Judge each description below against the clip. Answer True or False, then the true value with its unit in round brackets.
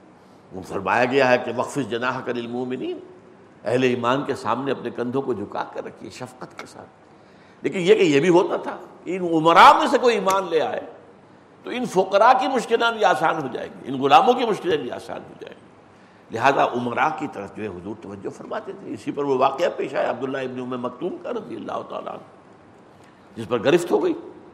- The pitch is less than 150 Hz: True (135 Hz)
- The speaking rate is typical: False (205 wpm)